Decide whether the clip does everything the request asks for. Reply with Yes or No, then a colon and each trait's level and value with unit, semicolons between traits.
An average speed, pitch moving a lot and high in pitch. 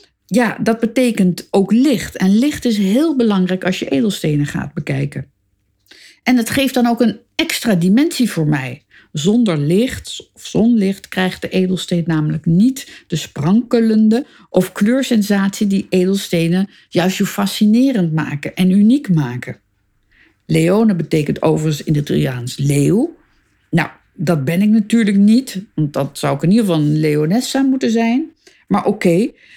Yes: average, 150 wpm; wide, 6.3 semitones; high, 195 Hz